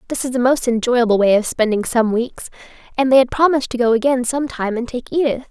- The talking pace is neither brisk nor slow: No, fast, 240 wpm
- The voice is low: No, high, 245 Hz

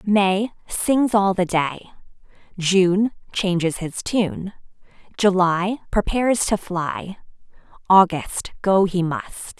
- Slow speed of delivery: Yes, slow, 80 wpm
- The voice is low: No, high, 190 Hz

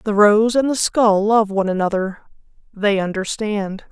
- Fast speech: No, average, 155 wpm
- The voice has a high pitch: Yes, high, 205 Hz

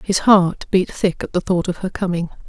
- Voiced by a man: No, female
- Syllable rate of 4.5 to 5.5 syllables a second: Yes, 5.0 syllables/s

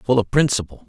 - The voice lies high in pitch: No, low, 120 Hz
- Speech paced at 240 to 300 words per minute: No, fast, 205 wpm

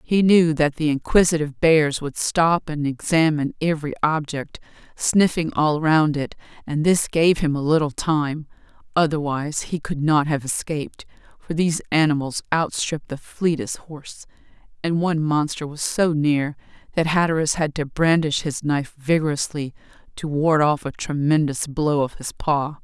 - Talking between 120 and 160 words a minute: Yes, average, 155 wpm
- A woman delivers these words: Yes, female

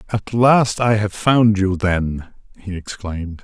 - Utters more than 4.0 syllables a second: No, 3.9 syllables/s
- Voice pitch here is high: No, low, 100 Hz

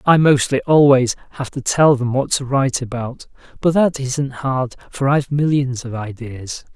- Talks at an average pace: Yes, average, 180 wpm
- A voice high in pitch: No, low, 135 Hz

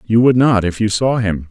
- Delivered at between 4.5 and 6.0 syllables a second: Yes, 5.0 syllables/s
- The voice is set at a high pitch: No, low, 110 Hz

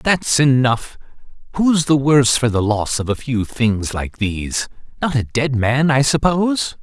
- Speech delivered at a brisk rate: No, average, 175 wpm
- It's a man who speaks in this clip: Yes, male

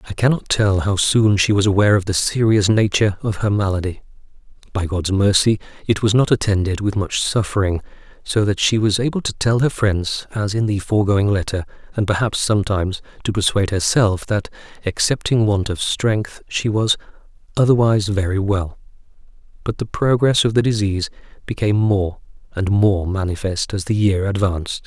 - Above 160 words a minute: Yes, average, 170 wpm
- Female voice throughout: No, male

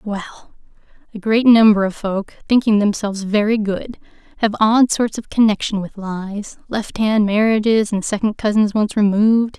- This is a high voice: Yes, high, 210 Hz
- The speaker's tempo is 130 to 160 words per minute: Yes, average, 155 wpm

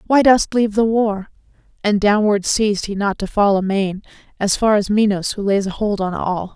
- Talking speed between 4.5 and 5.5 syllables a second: Yes, 4.9 syllables/s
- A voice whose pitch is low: No, high, 205 Hz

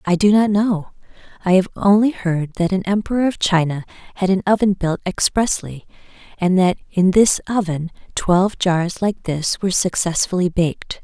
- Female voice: Yes, female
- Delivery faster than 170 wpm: No, average, 165 wpm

